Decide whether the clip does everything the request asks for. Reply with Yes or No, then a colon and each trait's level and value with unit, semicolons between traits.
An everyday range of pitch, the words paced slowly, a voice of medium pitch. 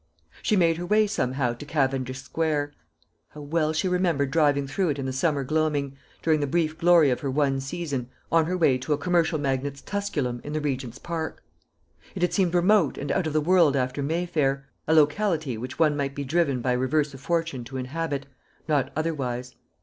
No: average, 3.6 semitones; average, 195 wpm; medium, 145 Hz